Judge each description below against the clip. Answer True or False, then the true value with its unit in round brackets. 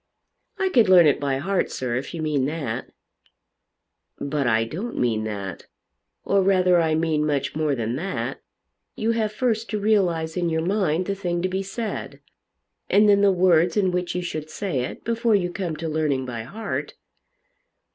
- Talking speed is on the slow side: False (180 wpm)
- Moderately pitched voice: True (175 Hz)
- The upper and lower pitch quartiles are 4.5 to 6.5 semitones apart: True (5.2 semitones)